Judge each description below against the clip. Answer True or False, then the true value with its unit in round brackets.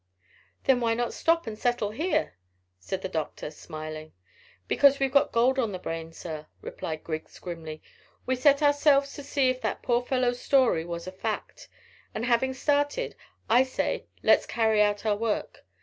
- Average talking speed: True (175 wpm)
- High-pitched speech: True (235 Hz)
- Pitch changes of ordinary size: False (7.5 semitones)